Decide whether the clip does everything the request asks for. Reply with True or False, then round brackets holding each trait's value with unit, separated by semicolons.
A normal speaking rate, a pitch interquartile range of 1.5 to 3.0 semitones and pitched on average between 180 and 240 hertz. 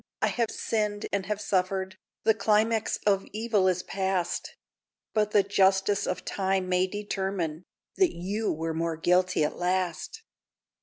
True (145 wpm; 2.4 semitones; 190 Hz)